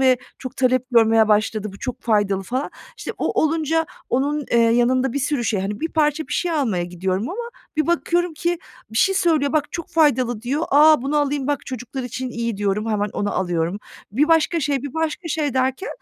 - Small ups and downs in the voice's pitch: No, wide, 5.5 semitones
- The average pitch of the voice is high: Yes, very high, 260 Hz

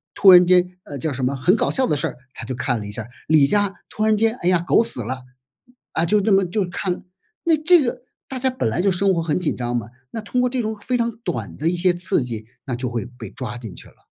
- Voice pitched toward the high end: No, medium, 175 Hz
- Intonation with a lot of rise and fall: Yes, wide, 8.9 semitones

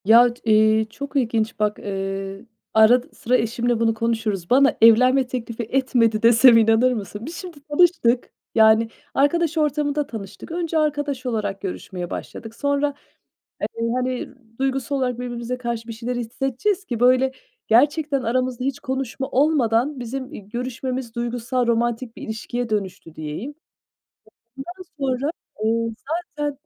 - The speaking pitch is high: Yes, high, 245 Hz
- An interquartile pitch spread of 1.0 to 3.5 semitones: Yes, average, 3.2 semitones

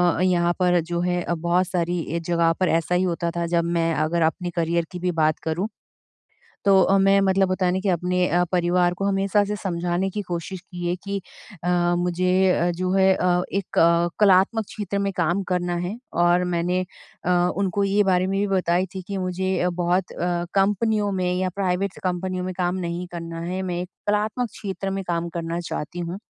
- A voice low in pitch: No, medium, 180 Hz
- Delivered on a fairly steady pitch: Yes, narrow, 1.8 semitones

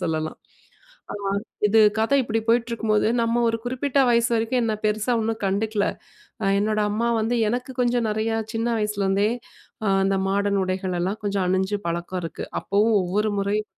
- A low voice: No, high, 215 Hz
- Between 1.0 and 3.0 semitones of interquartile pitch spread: Yes, average, 2.7 semitones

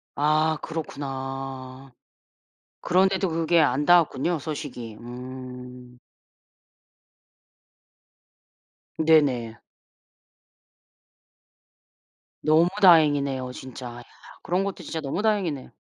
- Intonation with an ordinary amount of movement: Yes, average, 4.1 semitones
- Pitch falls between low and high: Yes, medium, 145 Hz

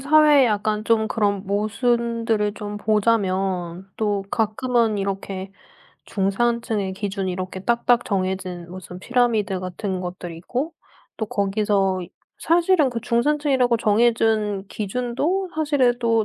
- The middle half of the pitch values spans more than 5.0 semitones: No, average, 3.7 semitones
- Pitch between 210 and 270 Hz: Yes, high, 215 Hz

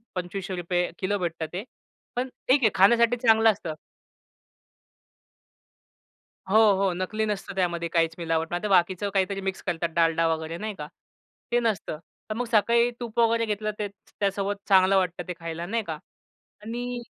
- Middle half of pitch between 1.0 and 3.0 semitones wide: No, average, 4.0 semitones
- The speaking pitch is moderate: No, high, 195 Hz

